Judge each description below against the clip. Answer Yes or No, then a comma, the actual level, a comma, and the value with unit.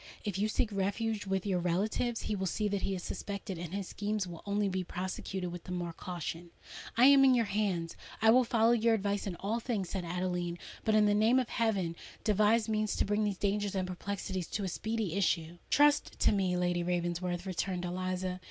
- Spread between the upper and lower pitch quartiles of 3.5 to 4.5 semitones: No, average, 3.1 semitones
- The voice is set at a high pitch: Yes, high, 195 Hz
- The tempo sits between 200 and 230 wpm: Yes, fast, 205 wpm